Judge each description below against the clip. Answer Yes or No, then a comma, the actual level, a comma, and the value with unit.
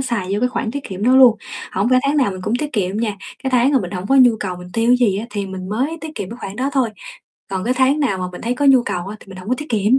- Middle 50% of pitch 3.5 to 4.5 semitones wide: No, average, 5.1 semitones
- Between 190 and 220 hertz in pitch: No, high, 230 Hz